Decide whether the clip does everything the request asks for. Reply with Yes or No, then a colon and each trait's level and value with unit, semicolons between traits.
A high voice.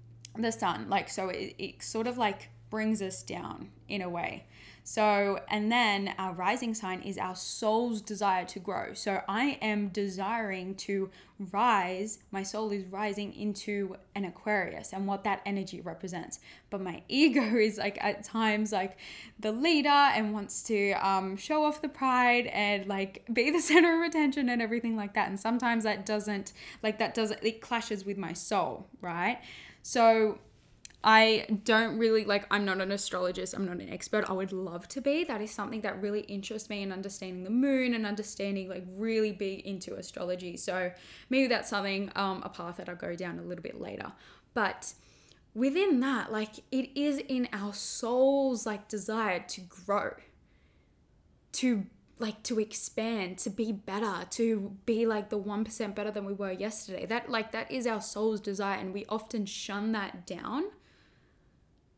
Yes: high, 210 Hz